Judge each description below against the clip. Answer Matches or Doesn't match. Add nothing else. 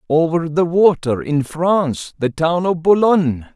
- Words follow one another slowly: Matches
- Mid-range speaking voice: Matches